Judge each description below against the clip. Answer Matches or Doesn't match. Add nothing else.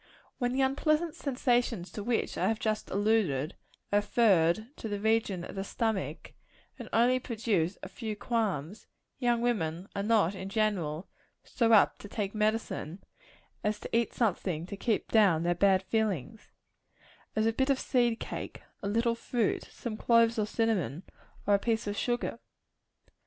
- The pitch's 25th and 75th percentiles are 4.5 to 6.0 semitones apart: Doesn't match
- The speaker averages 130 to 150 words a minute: Doesn't match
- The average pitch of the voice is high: Matches